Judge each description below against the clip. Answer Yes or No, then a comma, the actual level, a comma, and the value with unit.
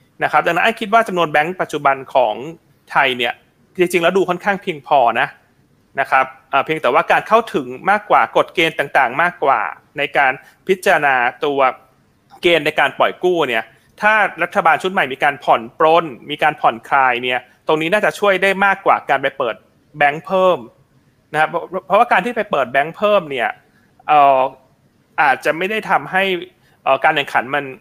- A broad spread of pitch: Yes, wide, 5.9 semitones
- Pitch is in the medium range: Yes, medium, 165 Hz